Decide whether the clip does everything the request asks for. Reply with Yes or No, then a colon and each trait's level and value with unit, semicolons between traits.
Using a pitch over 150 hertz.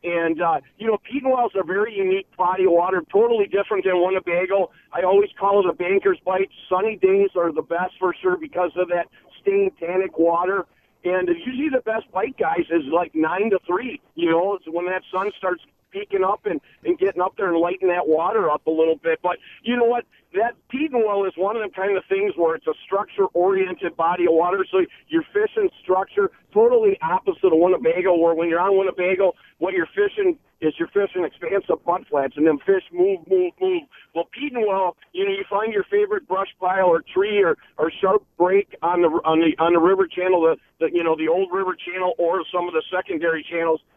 Yes: high, 190 Hz